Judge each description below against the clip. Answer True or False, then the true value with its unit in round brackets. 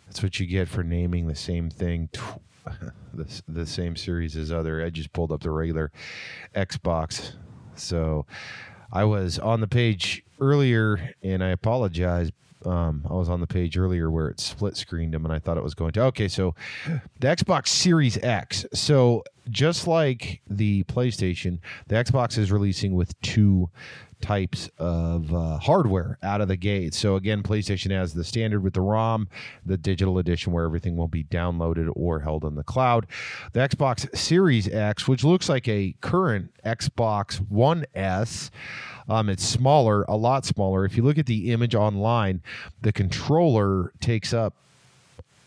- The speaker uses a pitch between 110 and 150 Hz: False (100 Hz)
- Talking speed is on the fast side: False (170 wpm)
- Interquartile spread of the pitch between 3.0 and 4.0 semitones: False (4.8 semitones)